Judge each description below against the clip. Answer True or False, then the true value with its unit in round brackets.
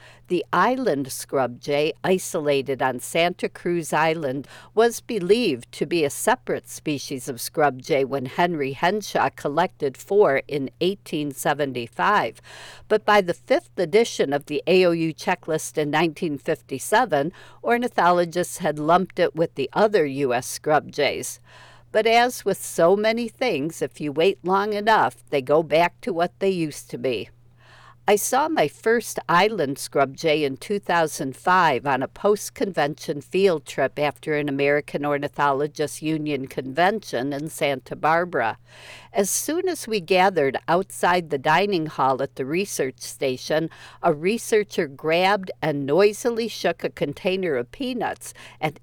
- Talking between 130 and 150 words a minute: True (145 wpm)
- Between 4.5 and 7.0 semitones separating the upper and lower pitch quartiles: True (5.3 semitones)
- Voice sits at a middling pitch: True (160 Hz)